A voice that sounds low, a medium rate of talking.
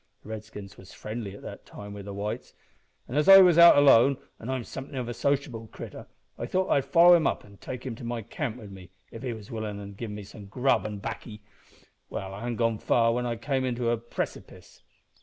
No: low, 115 Hz; fast, 230 wpm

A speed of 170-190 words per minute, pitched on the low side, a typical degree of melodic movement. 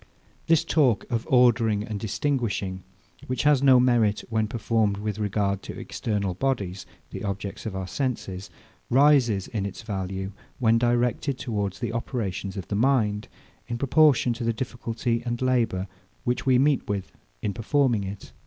No: average, 155 wpm; low, 115 Hz; average, 3.9 semitones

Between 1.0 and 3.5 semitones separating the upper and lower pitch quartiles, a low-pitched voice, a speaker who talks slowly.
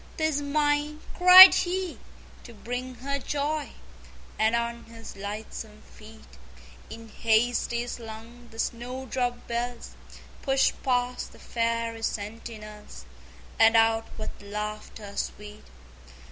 No: average, 2.9 semitones; high, 235 Hz; slow, 110 wpm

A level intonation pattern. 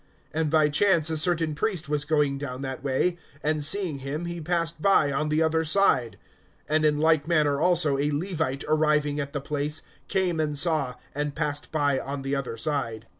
Yes: narrow, 2.3 semitones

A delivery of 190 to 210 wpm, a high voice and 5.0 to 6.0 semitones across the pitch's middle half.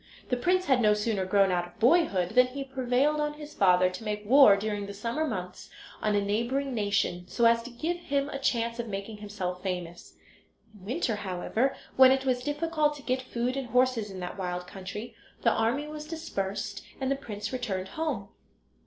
Yes: average, 195 wpm; high, 230 Hz; average, 5.3 semitones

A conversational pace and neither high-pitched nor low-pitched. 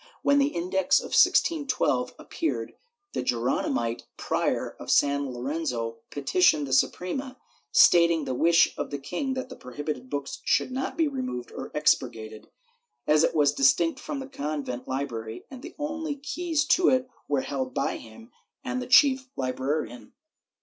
Yes: average, 155 wpm; medium, 160 Hz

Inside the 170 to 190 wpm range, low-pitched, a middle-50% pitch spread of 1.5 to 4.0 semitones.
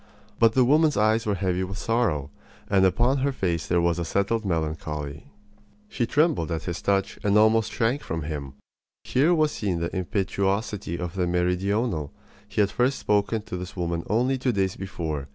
No: average, 180 wpm; low, 100 Hz; average, 4.8 semitones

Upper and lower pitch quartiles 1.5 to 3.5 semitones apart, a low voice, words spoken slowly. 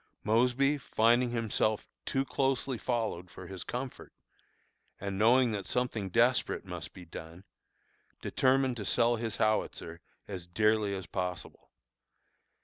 No: average, 4.4 semitones; low, 110 Hz; slow, 125 wpm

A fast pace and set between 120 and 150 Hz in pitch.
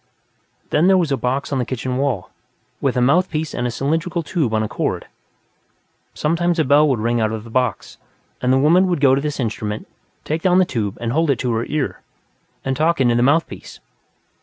Yes: fast, 210 wpm; low, 135 Hz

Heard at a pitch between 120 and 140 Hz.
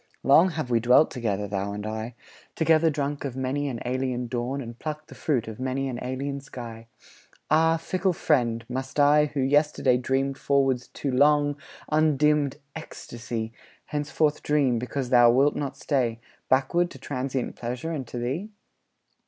Yes: low, 135 Hz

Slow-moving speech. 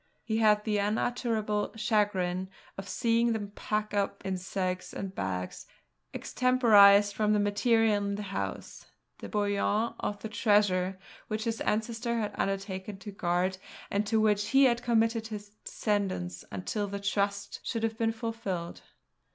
No: average, 150 wpm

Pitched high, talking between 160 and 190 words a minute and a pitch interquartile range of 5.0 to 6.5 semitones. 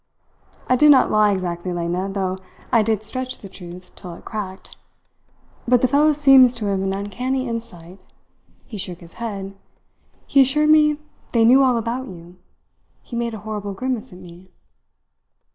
Yes: high, 215 Hz; average, 165 wpm; wide, 5.4 semitones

